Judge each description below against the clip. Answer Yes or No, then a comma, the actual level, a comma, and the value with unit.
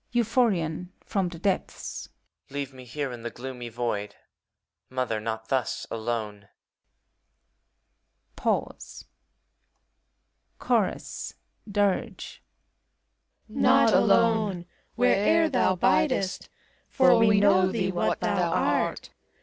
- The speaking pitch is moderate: Yes, medium, 175 Hz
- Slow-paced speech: Yes, slow, 95 wpm